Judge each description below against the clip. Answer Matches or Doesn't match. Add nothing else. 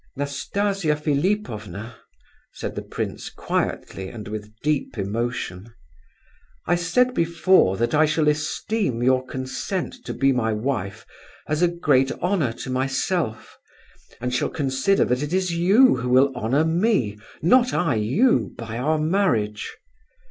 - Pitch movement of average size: Doesn't match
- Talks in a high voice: Doesn't match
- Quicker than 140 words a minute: Doesn't match